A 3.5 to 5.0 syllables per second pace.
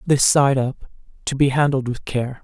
Yes: 4.6 syllables/s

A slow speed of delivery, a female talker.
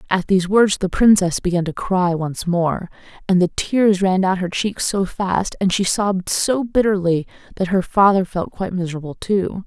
No: average, 190 wpm; female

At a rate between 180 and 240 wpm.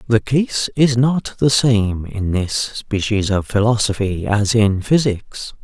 No: average, 150 wpm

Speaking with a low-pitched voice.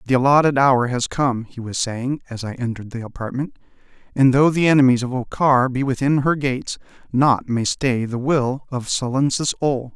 Yes: low, 130 Hz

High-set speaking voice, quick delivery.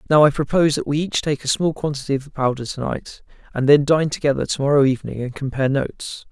No: medium, 140 Hz; fast, 240 wpm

